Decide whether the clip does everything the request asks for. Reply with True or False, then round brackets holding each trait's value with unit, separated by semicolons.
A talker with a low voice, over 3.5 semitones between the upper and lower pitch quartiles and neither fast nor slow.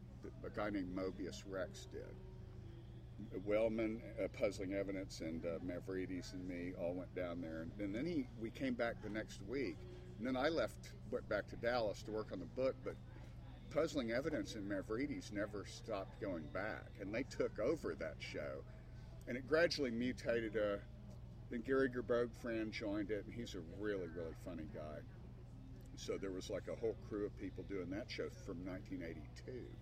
True (105 Hz; 4.3 semitones; 180 wpm)